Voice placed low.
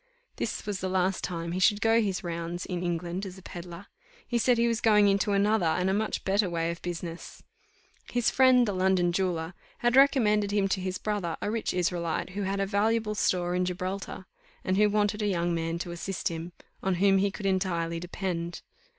No: high, 190 Hz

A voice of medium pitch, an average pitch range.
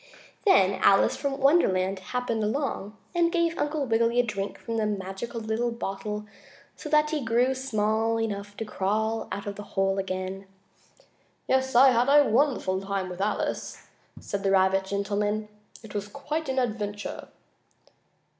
No: high, 215 Hz; average, 4.7 semitones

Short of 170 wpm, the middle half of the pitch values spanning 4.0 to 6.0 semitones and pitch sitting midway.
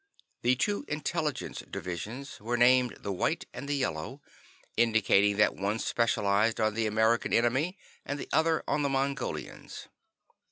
No: average, 145 wpm; average, 4.6 semitones; low, 120 Hz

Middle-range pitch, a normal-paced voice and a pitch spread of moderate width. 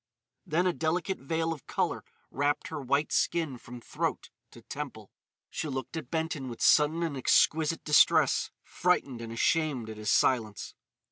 Yes: medium, 150 Hz; average, 155 wpm; average, 4.2 semitones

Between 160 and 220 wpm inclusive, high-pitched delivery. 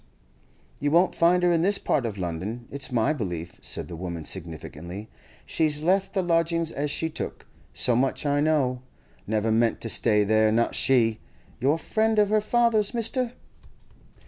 No: average, 170 wpm; medium, 140 Hz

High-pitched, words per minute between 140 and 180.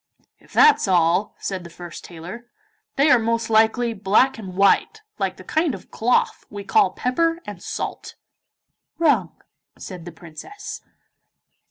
Yes: high, 215 Hz; average, 145 wpm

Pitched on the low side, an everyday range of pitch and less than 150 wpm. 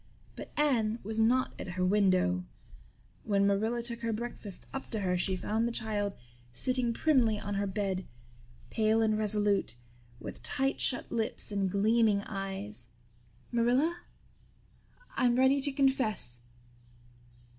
No: high, 215 Hz; average, 3.3 semitones; slow, 135 wpm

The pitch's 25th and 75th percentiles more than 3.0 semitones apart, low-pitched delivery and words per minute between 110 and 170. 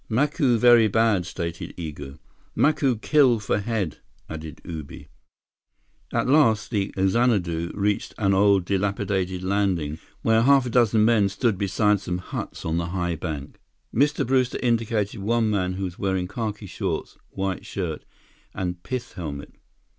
Yes: average, 4.4 semitones; low, 100 Hz; average, 145 wpm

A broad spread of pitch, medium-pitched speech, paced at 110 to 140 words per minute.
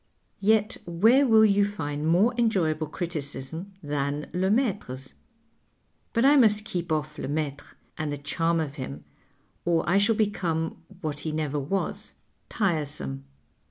Yes: wide, 5.7 semitones; medium, 165 Hz; slow, 135 wpm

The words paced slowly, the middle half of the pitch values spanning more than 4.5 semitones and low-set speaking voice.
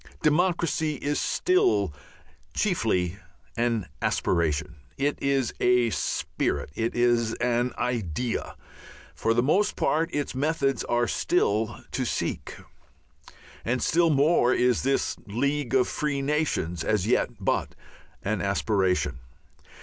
Yes: slow, 115 wpm; average, 5.2 semitones; low, 125 Hz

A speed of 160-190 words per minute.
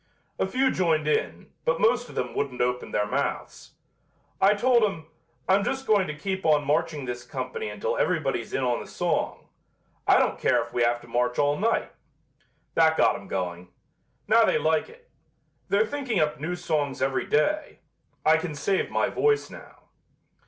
Yes: average, 180 wpm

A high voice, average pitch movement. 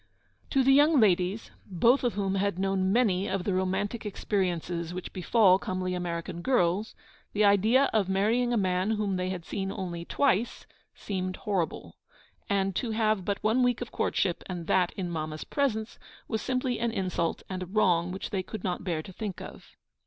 Yes: high, 195 Hz; average, 3.2 semitones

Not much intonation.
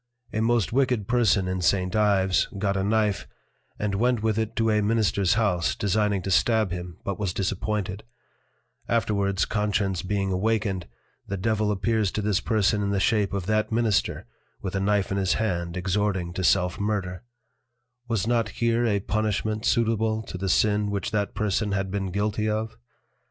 Yes: narrow, 2.3 semitones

